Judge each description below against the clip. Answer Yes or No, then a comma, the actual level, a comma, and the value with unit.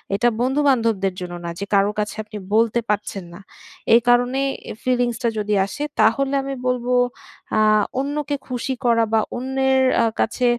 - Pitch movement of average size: Yes, average, 3.9 semitones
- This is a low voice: No, high, 240 Hz